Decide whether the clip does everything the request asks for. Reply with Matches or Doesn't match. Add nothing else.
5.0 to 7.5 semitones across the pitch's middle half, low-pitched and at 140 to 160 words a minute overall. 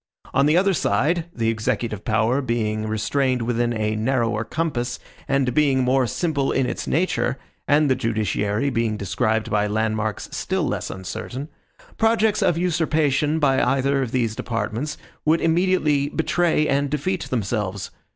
Matches